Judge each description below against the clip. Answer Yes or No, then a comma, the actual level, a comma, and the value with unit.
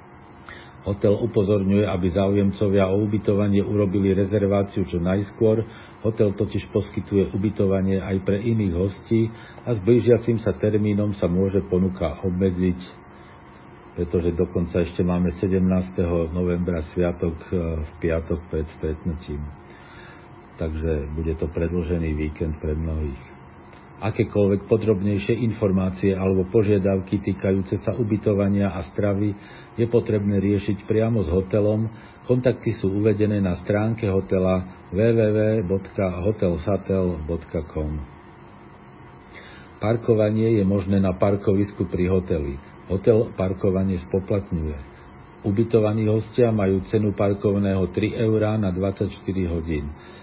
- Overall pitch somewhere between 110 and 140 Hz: No, very low, 95 Hz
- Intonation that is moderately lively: Yes, average, 3.0 semitones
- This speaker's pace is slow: Yes, slow, 105 wpm